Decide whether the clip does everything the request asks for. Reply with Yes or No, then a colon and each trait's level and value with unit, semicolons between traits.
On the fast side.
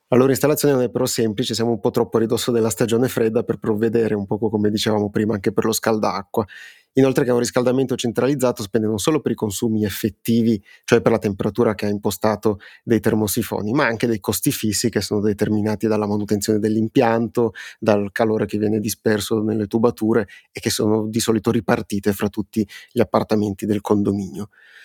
Yes: fast, 190 wpm